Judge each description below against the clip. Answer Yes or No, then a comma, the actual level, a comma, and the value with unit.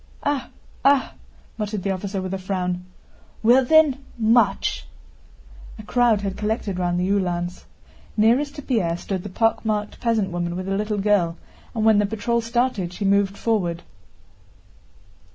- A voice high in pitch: Yes, high, 205 Hz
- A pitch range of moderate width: Yes, average, 3.7 semitones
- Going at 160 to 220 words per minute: No, average, 150 wpm